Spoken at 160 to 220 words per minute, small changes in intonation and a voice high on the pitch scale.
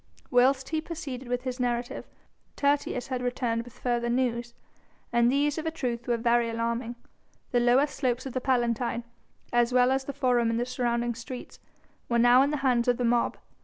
Yes: average, 190 wpm; narrow, 1.7 semitones; high, 245 Hz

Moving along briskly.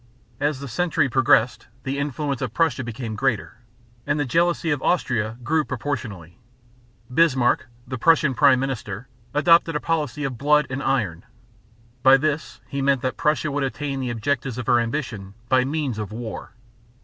No: average, 160 wpm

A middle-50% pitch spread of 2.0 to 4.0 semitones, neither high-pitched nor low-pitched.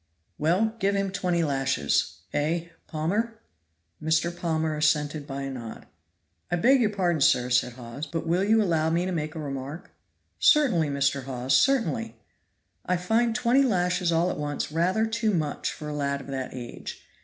No: wide, 5.5 semitones; medium, 165 Hz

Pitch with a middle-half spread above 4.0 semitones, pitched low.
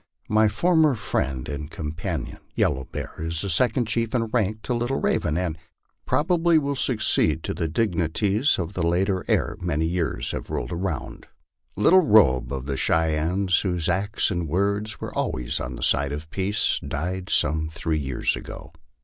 Yes: wide, 5.5 semitones; very low, 90 Hz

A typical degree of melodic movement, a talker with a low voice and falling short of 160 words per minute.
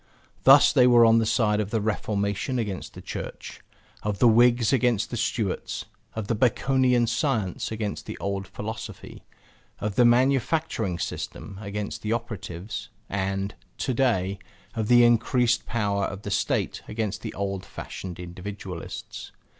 Yes: average, 3.3 semitones; low, 110 Hz; average, 145 wpm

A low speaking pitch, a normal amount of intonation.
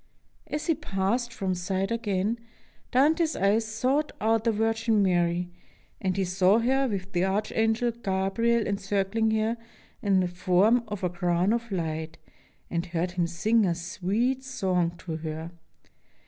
No: high, 195 Hz; average, 4.2 semitones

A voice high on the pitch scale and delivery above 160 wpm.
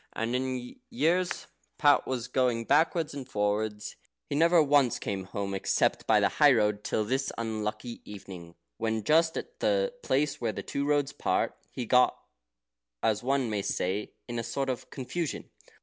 No: low, 125 Hz; average, 175 wpm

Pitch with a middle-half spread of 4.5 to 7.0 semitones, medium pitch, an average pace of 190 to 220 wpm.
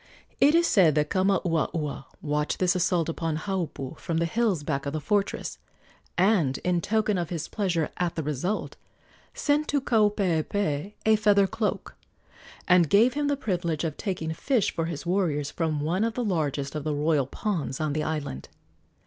No: average, 5.1 semitones; medium, 170 Hz; average, 175 wpm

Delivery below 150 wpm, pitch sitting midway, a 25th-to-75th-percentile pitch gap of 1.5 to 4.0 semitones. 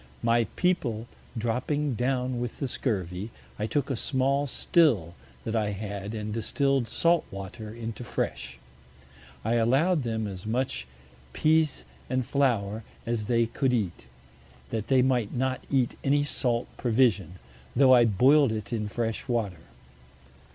No: average, 140 wpm; low, 120 Hz; average, 3.7 semitones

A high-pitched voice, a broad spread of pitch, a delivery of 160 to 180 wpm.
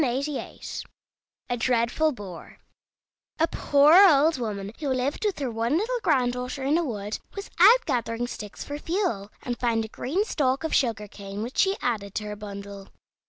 Yes: very high, 250 Hz; wide, 5.9 semitones; average, 165 wpm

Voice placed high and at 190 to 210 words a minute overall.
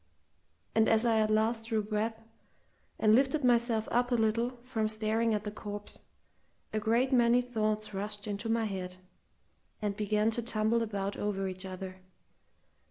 No: high, 220 Hz; average, 160 wpm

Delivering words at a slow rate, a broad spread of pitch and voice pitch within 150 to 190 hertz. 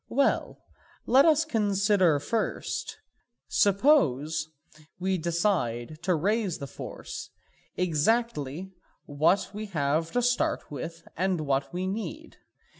Yes: slow, 110 wpm; wide, 5.8 semitones; medium, 185 Hz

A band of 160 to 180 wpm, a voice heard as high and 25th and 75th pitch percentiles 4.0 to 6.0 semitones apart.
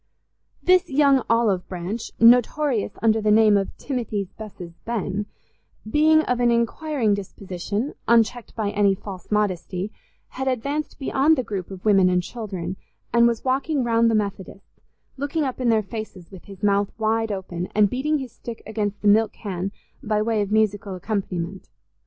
No: average, 165 wpm; high, 215 Hz; average, 3.6 semitones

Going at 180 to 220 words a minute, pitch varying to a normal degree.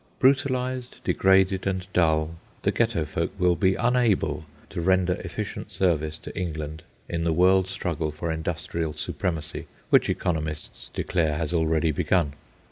No: slow, 135 wpm; average, 3.1 semitones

